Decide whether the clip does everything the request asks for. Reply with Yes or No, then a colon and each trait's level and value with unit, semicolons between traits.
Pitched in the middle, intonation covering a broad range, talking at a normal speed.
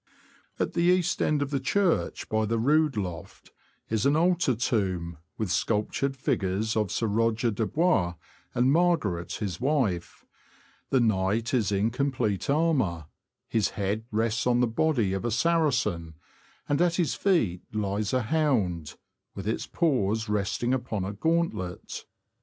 No: low, 115 Hz; wide, 6.3 semitones; average, 150 wpm